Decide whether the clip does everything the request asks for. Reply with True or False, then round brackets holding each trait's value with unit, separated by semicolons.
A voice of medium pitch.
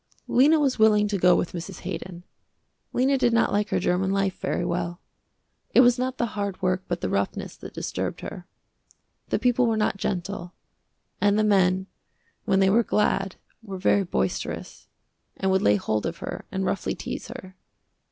False (195 Hz)